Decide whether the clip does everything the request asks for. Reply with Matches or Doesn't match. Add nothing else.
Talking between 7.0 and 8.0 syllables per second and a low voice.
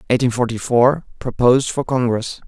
Matches